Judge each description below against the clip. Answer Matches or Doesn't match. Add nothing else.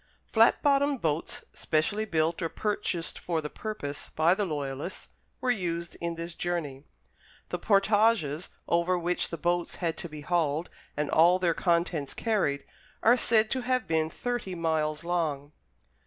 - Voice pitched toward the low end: Doesn't match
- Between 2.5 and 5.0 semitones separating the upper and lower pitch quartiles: Matches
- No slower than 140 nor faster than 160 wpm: Matches